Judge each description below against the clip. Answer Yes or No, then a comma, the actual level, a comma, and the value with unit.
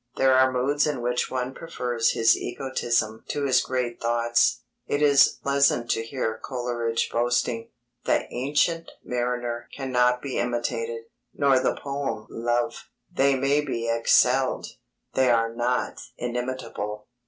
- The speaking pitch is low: Yes, low, 125 Hz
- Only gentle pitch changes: Yes, narrow, 2.1 semitones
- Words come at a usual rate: No, slow, 130 wpm